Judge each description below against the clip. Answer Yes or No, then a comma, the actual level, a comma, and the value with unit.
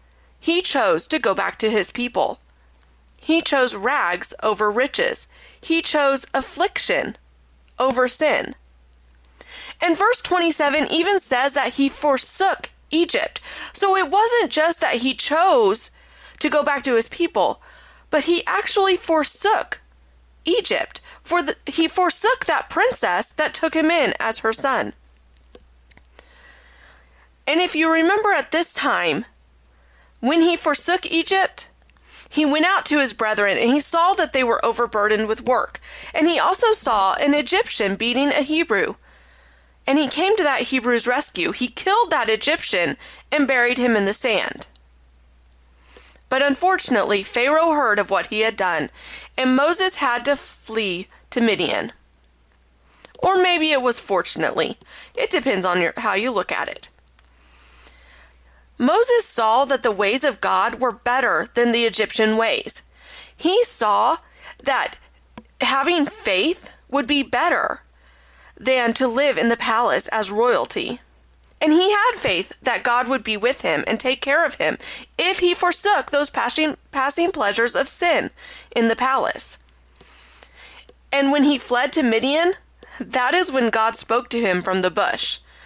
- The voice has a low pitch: No, very high, 270 Hz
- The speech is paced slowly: No, average, 150 wpm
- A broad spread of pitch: Yes, wide, 7.5 semitones